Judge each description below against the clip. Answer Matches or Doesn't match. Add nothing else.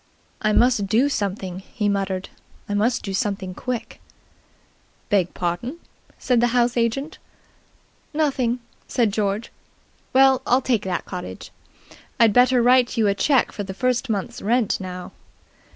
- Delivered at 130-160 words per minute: Matches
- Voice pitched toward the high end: Matches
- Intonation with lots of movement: Doesn't match